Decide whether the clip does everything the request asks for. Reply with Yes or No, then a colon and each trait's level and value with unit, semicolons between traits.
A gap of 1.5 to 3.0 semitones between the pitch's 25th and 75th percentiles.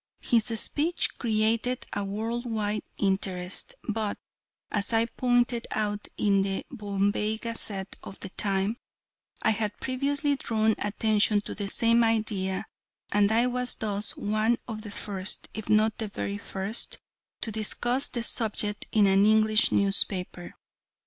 Yes: narrow, 2.4 semitones